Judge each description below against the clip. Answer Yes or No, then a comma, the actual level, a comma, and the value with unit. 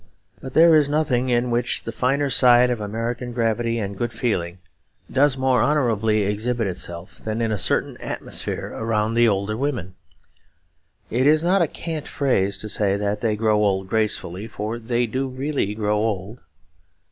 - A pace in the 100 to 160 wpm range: No, average, 170 wpm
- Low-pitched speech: Yes, low, 115 Hz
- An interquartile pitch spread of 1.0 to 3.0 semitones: No, average, 3.5 semitones